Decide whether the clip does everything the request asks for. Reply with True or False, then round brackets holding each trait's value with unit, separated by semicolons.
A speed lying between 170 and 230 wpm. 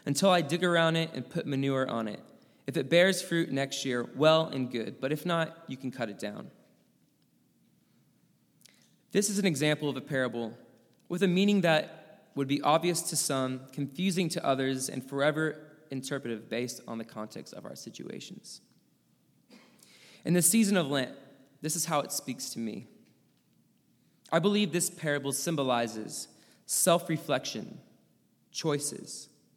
False (155 wpm)